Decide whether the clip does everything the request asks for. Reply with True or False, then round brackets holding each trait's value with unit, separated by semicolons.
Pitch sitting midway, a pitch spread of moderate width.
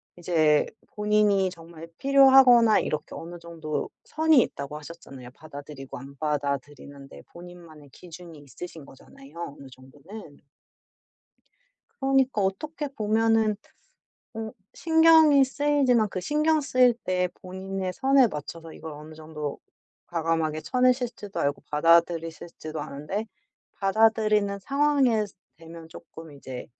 False (175 Hz; 6.9 semitones)